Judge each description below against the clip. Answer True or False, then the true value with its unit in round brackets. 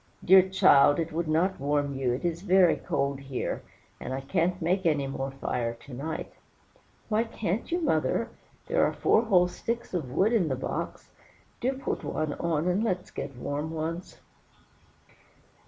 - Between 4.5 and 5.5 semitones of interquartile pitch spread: True (5.2 semitones)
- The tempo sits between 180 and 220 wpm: False (170 wpm)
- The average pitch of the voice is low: False (165 Hz)